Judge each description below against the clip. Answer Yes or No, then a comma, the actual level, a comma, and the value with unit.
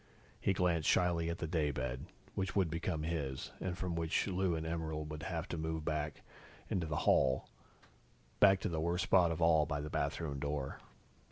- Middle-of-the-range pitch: No, very low, 80 Hz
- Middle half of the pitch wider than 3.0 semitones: No, narrow, 2.4 semitones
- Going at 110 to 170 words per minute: No, average, 185 wpm